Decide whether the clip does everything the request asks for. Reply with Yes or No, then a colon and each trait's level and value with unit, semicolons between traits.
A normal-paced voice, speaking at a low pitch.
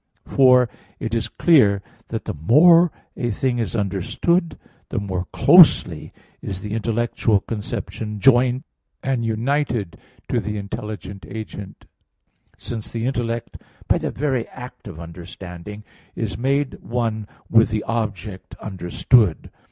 No: slow, 125 wpm; low, 110 Hz